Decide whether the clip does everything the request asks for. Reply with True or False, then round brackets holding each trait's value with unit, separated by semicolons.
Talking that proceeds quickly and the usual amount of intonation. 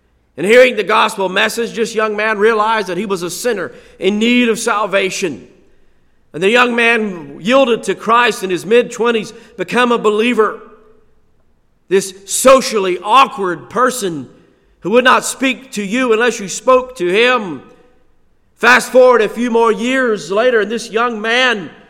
False (155 wpm; 3.2 semitones)